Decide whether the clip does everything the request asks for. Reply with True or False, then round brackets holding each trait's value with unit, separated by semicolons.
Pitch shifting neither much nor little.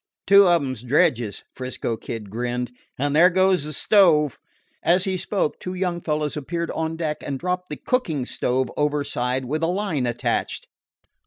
False (5.7 semitones)